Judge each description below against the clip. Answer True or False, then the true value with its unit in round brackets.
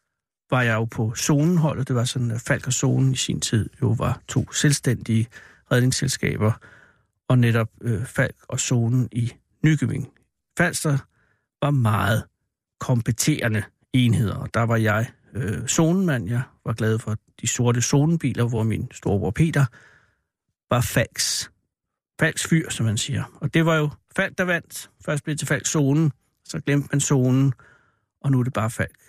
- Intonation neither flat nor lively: True (3.7 semitones)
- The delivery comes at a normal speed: True (165 wpm)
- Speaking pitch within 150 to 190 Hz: False (130 Hz)